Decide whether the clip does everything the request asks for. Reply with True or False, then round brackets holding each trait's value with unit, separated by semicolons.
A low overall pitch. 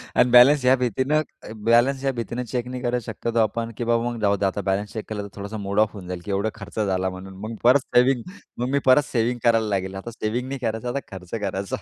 True (115 Hz)